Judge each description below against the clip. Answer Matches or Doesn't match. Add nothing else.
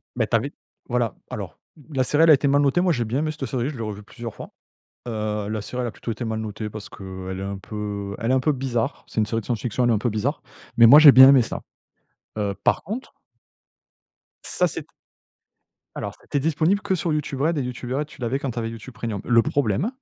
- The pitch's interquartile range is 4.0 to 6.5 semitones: Matches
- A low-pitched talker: Matches